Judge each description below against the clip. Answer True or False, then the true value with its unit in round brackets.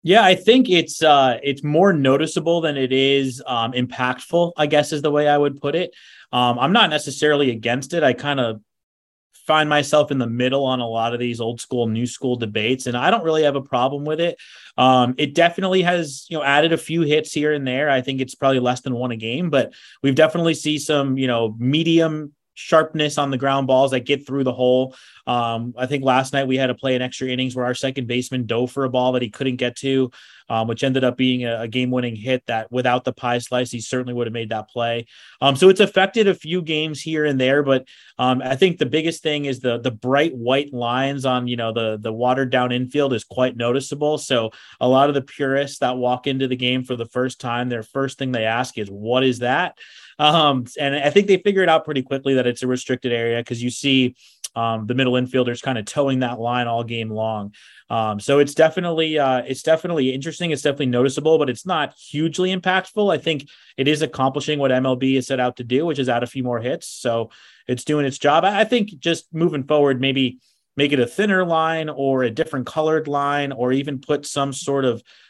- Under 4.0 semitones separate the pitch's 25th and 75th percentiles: True (3.3 semitones)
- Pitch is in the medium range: False (130 Hz)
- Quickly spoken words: True (230 wpm)